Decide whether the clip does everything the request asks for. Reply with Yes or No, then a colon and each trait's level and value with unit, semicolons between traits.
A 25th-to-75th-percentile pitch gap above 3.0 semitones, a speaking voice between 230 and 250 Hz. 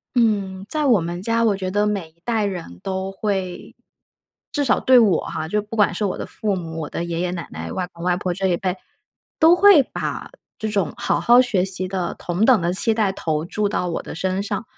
No: average, 3.4 semitones; high, 195 Hz